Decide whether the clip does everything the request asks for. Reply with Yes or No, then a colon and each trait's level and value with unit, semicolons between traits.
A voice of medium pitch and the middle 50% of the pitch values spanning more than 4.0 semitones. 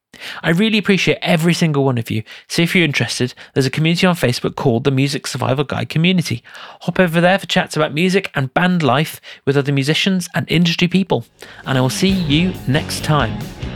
Yes: medium, 160 Hz; average, 4.7 semitones